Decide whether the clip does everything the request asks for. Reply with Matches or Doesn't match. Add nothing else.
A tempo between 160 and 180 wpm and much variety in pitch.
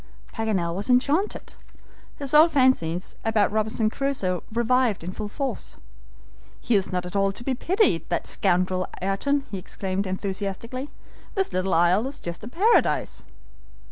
Doesn't match